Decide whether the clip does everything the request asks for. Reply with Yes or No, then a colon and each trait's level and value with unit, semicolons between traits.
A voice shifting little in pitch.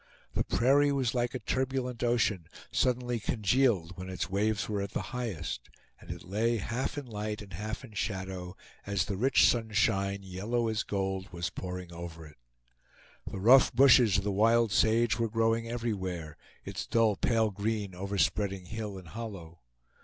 No: average, 3.7 semitones